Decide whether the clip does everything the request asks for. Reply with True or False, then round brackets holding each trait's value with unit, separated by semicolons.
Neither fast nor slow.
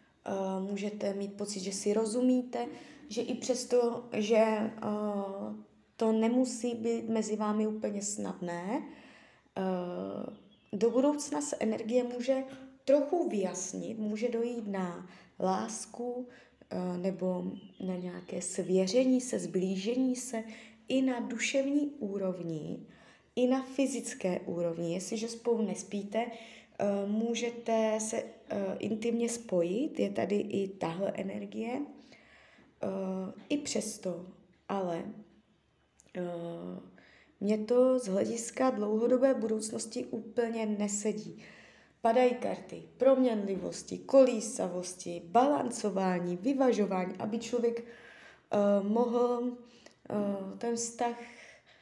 False (95 wpm)